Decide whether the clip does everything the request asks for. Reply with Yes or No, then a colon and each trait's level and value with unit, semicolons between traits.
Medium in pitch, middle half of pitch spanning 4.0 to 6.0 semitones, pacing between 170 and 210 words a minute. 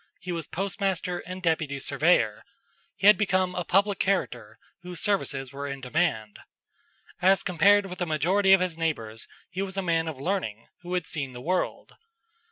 Yes: medium, 180 Hz; average, 4.4 semitones; average, 175 wpm